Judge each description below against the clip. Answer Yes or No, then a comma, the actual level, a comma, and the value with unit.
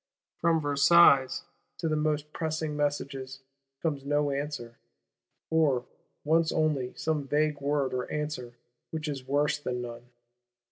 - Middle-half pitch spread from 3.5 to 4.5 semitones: No, narrow, 2.4 semitones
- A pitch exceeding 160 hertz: No, medium, 145 Hz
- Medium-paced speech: No, slow, 130 wpm